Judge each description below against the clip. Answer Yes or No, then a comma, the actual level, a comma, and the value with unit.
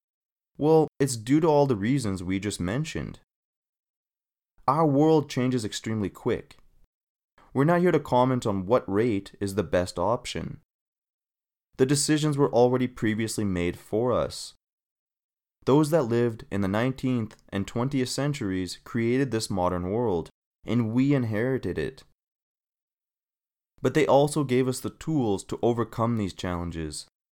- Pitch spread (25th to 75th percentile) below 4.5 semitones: No, wide, 5.4 semitones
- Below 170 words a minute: Yes, average, 140 wpm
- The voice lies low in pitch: Yes, low, 120 Hz